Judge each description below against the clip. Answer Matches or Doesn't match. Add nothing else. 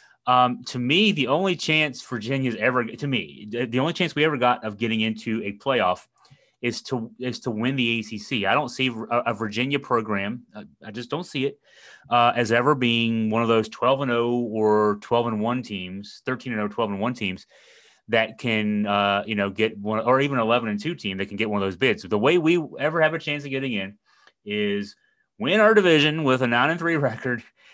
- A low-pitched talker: Matches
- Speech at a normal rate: Doesn't match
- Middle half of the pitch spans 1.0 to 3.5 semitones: Doesn't match